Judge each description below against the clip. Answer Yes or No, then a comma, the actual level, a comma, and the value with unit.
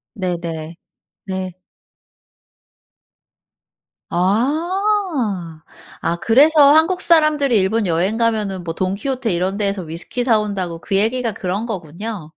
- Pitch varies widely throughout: Yes, wide, 6.1 semitones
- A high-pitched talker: Yes, high, 205 Hz